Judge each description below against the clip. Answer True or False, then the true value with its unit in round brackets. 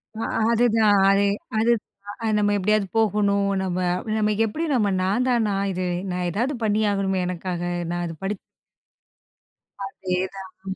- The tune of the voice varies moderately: False (2.2 semitones)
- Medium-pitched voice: False (200 Hz)